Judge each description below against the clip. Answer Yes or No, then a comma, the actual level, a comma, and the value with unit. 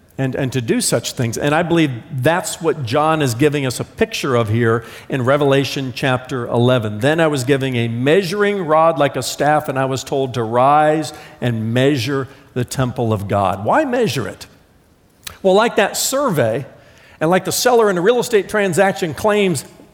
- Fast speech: No, average, 185 wpm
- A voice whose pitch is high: No, medium, 140 Hz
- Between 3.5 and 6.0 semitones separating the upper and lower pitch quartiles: Yes, average, 4.5 semitones